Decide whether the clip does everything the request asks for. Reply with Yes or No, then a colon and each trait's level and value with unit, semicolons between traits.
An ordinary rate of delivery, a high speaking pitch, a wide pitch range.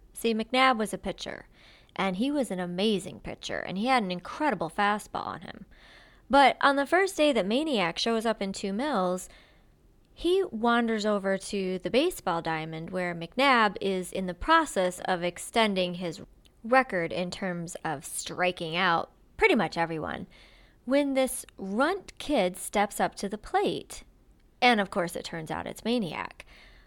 Yes: average, 165 wpm; high, 205 Hz; wide, 6.3 semitones